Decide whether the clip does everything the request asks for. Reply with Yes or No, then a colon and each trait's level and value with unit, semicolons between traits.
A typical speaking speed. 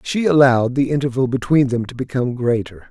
Yes: average, 185 wpm